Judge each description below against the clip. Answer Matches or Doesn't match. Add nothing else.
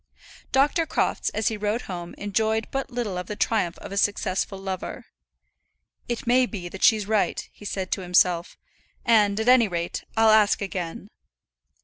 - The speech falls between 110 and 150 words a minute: Doesn't match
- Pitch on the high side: Matches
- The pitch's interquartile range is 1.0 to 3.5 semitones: Matches